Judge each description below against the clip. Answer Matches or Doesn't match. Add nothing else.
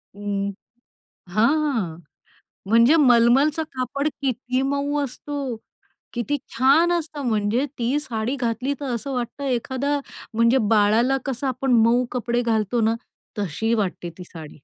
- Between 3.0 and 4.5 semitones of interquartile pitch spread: Matches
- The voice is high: Matches